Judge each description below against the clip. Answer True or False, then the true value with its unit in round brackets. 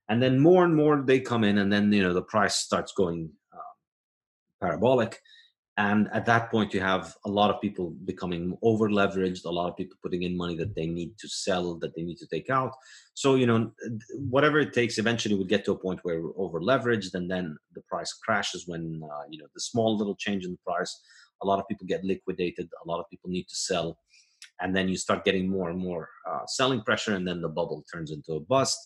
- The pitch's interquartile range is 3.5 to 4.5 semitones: True (4.2 semitones)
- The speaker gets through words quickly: True (235 wpm)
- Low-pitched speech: True (100 Hz)